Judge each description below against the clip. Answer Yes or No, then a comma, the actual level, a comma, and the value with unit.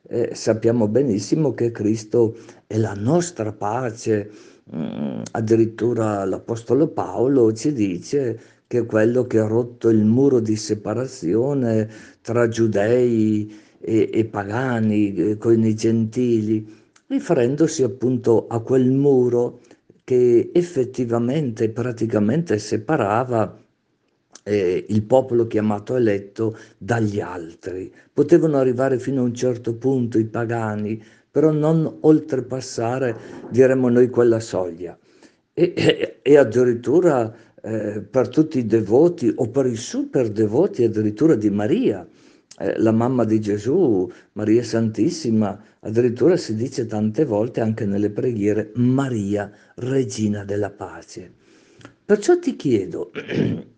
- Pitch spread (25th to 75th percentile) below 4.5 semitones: Yes, average, 2.9 semitones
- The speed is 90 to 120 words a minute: Yes, slow, 115 wpm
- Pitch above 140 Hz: No, low, 115 Hz